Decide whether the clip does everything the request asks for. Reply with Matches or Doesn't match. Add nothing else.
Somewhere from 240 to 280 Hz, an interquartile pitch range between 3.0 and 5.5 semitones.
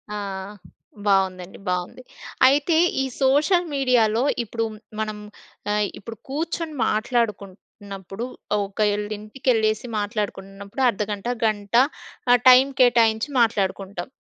Doesn't match